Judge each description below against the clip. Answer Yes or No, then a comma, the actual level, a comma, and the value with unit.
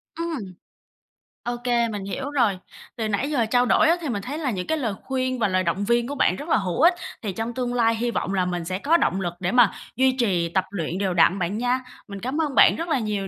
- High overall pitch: Yes, high, 230 Hz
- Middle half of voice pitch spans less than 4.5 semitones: No, average, 5.1 semitones